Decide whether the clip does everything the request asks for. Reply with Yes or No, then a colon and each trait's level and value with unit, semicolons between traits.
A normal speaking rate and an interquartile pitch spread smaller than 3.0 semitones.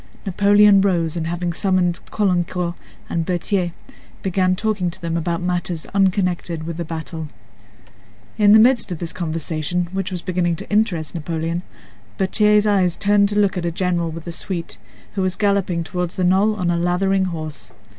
Yes: average, 170 wpm; narrow, 2.5 semitones